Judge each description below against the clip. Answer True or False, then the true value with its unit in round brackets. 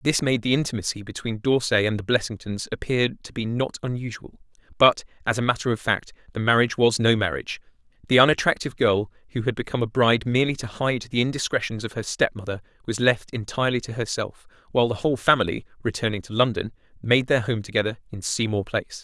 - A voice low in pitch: True (115 Hz)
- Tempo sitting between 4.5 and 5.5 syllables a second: False (6.5 syllables/s)